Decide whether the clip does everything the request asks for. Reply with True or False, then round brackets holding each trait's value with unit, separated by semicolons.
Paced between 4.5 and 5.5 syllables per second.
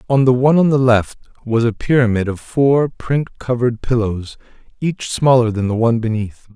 True (5.2 syllables/s)